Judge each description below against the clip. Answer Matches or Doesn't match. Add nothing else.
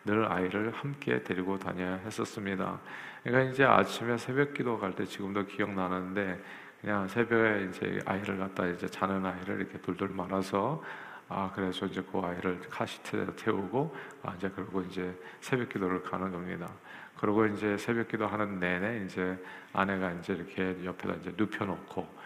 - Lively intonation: Doesn't match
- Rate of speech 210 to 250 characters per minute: Doesn't match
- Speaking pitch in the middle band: Doesn't match